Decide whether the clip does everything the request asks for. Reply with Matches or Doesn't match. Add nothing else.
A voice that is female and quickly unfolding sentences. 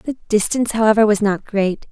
Doesn't match